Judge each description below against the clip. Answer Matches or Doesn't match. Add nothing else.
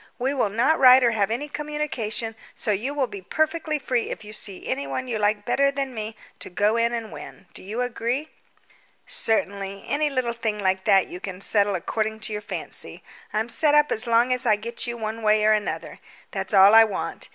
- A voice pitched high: Matches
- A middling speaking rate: Doesn't match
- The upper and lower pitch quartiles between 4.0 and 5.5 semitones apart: Doesn't match